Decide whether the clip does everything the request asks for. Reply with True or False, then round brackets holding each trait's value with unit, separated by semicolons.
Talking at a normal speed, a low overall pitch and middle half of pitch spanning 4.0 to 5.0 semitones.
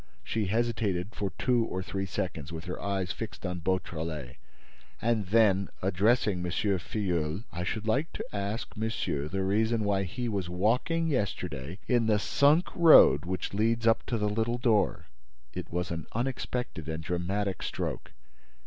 True (160 wpm; 100 Hz; 4.3 semitones)